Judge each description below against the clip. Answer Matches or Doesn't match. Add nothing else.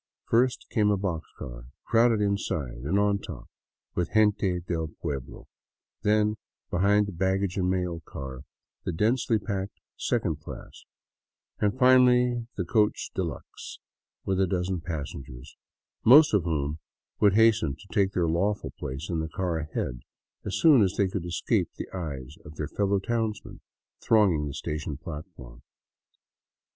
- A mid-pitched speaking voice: Doesn't match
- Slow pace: Doesn't match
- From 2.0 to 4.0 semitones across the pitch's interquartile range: Doesn't match